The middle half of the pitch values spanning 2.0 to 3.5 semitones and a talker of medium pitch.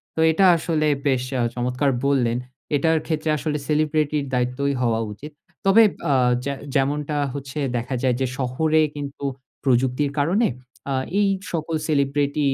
Yes: average, 2.8 semitones; medium, 145 Hz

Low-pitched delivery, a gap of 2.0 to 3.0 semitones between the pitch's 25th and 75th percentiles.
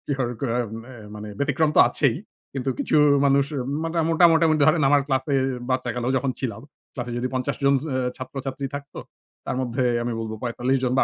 Yes: low, 130 Hz; narrow, 2.4 semitones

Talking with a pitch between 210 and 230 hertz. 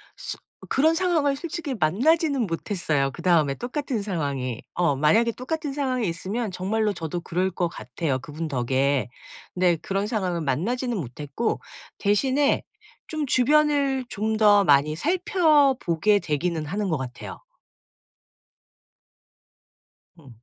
No: high, 200 Hz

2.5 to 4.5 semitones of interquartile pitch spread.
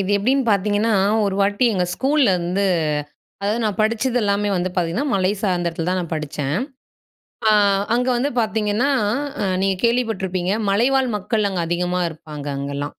Yes: average, 4.1 semitones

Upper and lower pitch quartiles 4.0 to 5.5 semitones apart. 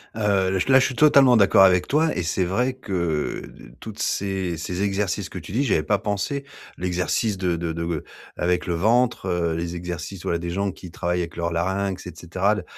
No: average, 3.1 semitones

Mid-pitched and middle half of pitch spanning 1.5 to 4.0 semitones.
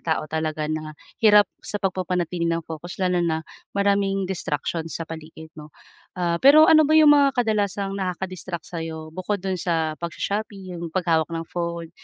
Yes: medium, 175 Hz; average, 3.4 semitones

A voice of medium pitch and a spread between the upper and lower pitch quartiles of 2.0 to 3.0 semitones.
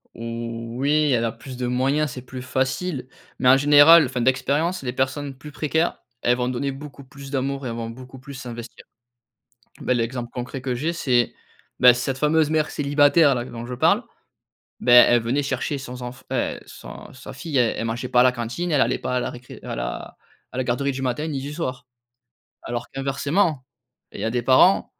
No: low, 130 Hz; average, 2.7 semitones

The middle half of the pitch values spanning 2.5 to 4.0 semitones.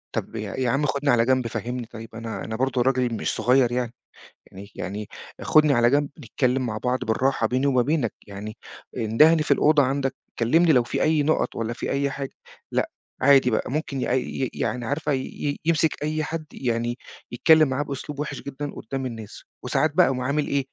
Yes: average, 3.4 semitones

